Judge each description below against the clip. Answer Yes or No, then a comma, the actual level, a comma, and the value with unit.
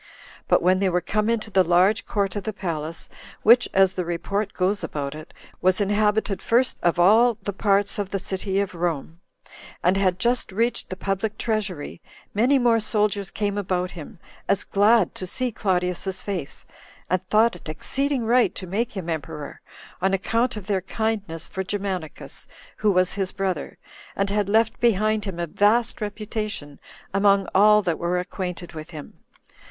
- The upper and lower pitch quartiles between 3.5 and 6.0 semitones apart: No, average, 2.9 semitones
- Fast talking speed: No, average, 170 wpm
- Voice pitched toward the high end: Yes, high, 195 Hz